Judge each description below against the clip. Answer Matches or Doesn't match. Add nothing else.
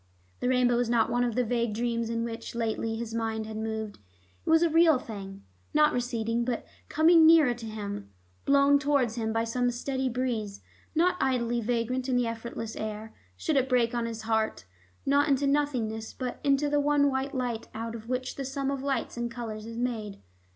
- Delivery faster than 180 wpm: Matches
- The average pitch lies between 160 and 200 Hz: Doesn't match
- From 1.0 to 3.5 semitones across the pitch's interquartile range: Matches